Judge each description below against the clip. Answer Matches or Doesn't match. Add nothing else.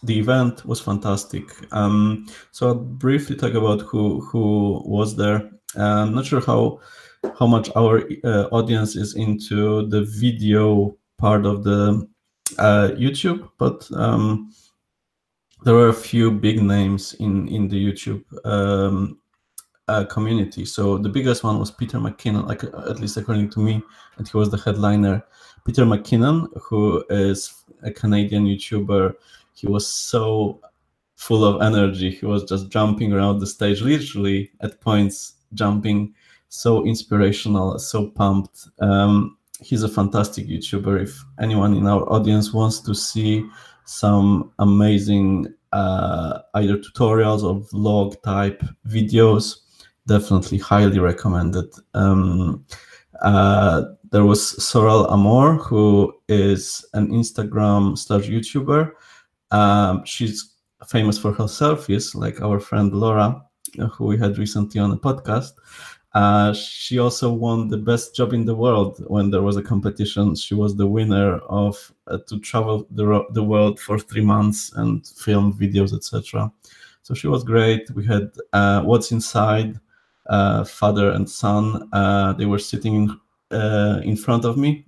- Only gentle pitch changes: Matches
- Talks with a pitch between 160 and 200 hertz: Doesn't match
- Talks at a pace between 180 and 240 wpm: Doesn't match